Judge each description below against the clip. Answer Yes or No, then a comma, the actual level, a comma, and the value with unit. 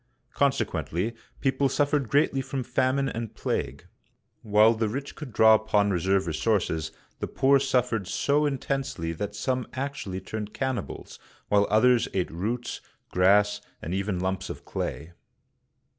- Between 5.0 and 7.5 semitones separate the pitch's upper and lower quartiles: Yes, average, 5.3 semitones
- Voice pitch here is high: No, low, 110 Hz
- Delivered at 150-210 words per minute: No, average, 140 wpm